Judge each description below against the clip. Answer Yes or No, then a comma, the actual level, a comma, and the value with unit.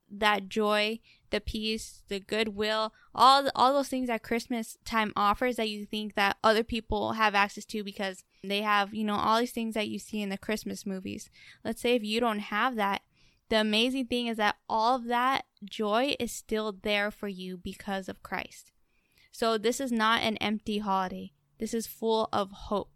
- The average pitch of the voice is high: Yes, high, 215 Hz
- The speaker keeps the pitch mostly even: Yes, narrow, 2.0 semitones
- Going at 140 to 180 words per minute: No, average, 195 wpm